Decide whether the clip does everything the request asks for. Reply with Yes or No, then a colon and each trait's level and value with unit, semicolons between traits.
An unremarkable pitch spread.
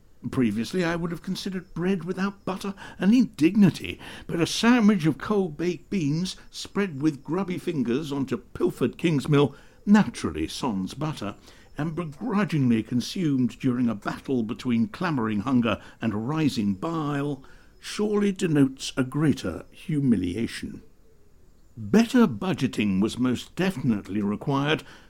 No: wide, 8.1 semitones